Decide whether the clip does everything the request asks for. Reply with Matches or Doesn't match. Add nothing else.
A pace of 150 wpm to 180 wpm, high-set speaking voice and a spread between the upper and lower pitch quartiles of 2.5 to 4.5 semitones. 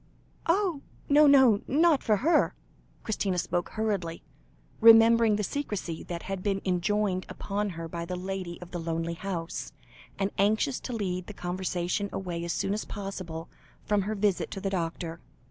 Matches